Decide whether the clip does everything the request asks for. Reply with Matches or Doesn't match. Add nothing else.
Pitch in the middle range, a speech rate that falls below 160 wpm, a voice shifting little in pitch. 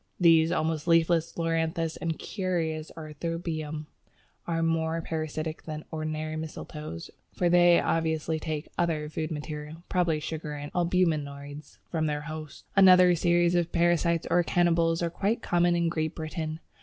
Matches